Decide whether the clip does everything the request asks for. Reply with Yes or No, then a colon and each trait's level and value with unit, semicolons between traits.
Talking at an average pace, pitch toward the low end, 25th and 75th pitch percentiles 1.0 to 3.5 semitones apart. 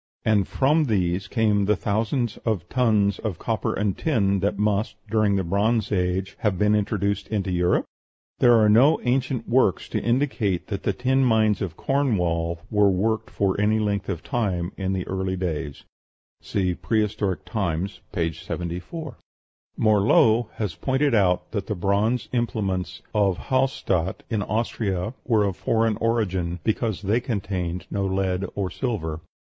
Yes: average, 150 wpm; low, 105 Hz; average, 3.2 semitones